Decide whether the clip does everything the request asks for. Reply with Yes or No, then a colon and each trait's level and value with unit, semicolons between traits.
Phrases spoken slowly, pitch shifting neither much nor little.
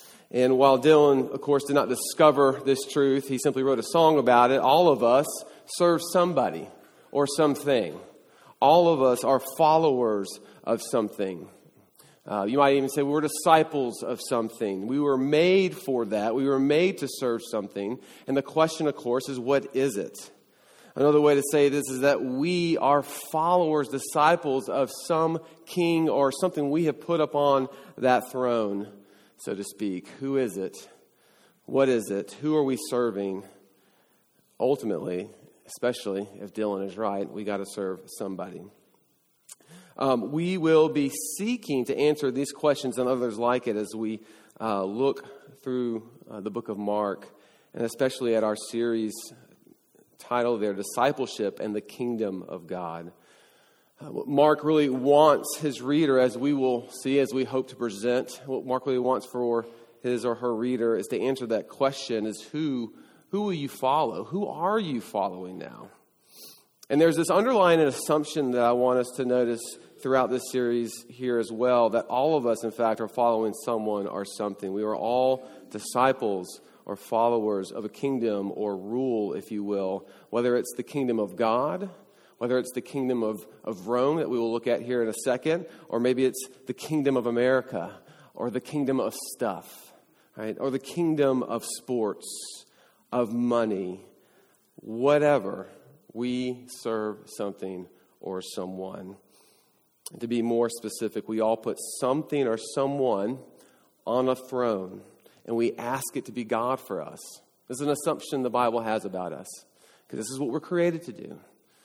No: average, 170 wpm; average, 3.9 semitones